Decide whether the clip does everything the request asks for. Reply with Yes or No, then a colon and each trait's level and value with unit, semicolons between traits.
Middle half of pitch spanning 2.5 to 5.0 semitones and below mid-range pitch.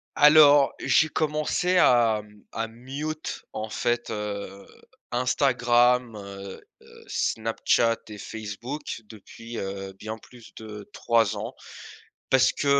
Yes: average, 3.6 semitones; low, 115 Hz